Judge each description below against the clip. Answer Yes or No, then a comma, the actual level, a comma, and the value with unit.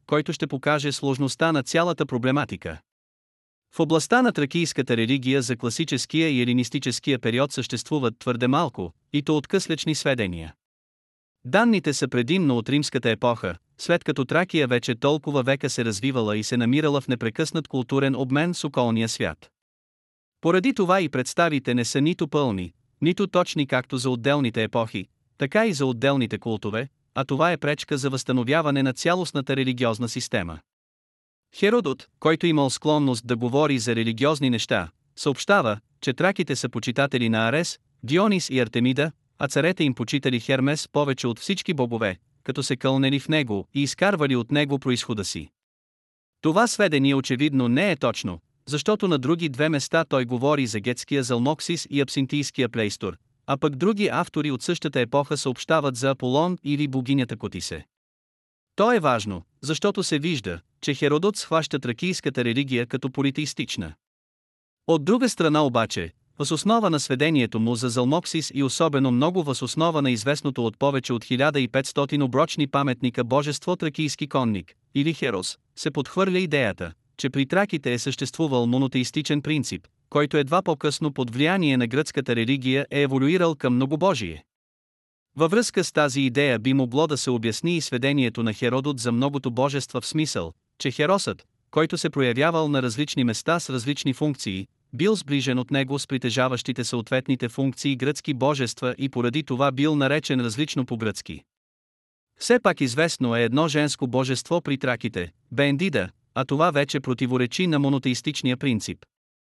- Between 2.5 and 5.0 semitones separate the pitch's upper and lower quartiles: Yes, average, 3.6 semitones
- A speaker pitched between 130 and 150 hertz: Yes, low, 135 Hz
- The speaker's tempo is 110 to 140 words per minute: No, average, 150 wpm